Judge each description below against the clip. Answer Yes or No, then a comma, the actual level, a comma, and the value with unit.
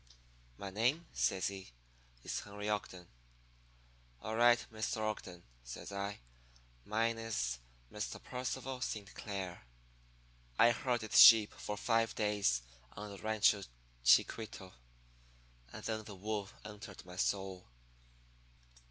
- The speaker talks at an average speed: No, slow, 115 wpm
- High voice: No, low, 105 Hz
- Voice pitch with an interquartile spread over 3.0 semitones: No, average, 2.7 semitones